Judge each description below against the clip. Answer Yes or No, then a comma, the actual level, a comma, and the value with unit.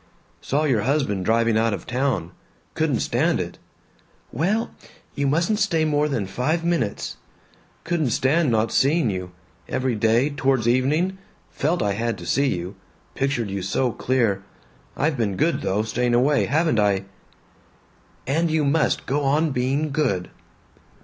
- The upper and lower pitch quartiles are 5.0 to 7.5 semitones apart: Yes, average, 5.3 semitones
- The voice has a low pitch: Yes, low, 130 Hz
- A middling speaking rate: Yes, average, 150 wpm